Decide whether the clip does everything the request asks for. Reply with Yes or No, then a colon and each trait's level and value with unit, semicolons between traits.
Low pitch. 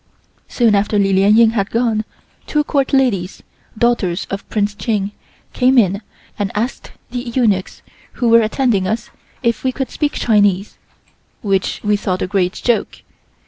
No: high, 215 Hz